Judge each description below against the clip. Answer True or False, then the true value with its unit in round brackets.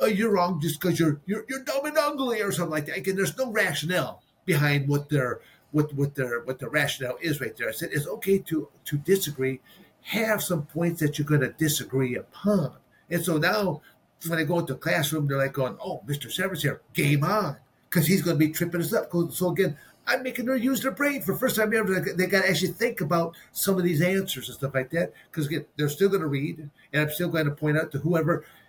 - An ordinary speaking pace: False (230 wpm)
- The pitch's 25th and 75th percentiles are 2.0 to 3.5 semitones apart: False (4.6 semitones)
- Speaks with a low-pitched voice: False (170 Hz)